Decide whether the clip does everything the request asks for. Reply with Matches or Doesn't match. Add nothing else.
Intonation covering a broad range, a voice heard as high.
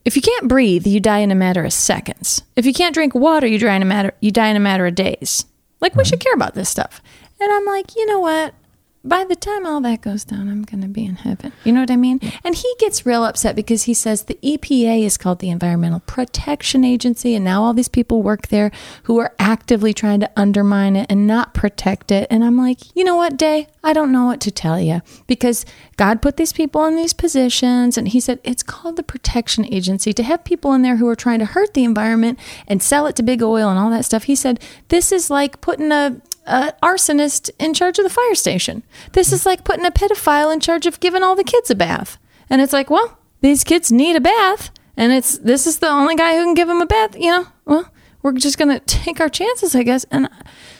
Matches